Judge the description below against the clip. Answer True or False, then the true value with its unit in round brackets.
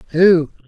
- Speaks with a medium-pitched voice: True (170 Hz)